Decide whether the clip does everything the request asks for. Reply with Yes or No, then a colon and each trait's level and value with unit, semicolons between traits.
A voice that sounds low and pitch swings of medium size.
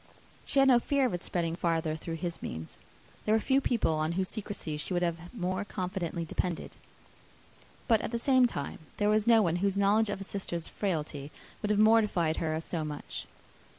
No: medium, 185 Hz; average, 4.7 semitones